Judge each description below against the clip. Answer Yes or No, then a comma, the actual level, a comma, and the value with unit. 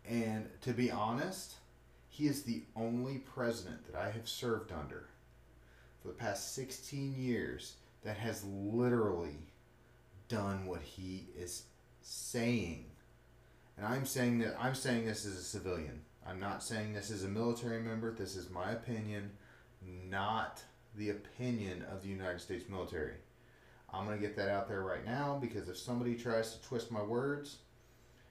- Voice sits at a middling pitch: No, low, 110 Hz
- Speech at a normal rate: Yes, average, 155 wpm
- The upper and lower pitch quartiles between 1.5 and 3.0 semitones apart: No, average, 4.1 semitones